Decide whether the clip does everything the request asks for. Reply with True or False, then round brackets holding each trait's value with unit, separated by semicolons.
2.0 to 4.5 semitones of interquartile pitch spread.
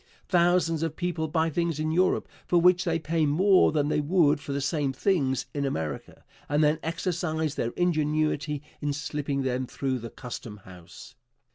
True (3.1 semitones)